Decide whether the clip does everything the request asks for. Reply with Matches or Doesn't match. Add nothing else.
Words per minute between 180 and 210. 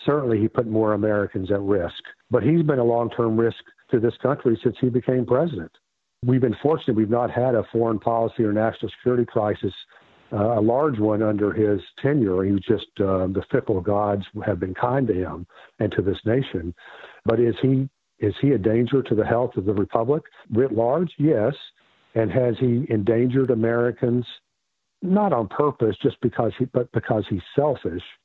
Matches